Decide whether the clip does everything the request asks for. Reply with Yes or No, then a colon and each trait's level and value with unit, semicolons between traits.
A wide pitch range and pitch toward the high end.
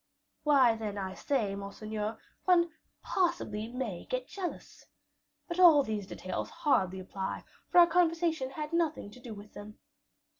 Yes: wide, 8.4 semitones; very high, 250 Hz